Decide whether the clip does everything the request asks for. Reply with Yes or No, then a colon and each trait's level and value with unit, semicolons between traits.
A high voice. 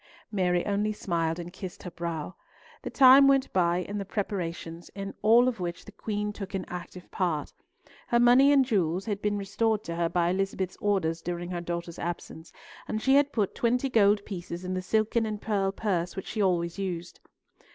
Yes: high, 195 Hz